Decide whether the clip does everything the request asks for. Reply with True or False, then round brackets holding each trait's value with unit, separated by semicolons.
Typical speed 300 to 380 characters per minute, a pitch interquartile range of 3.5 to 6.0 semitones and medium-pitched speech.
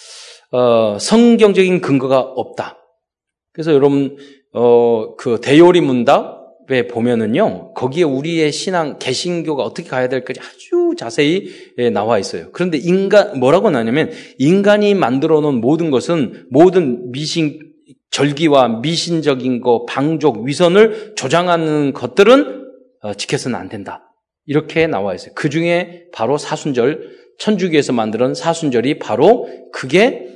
False (285 characters per minute; 5.4 semitones; 155 Hz)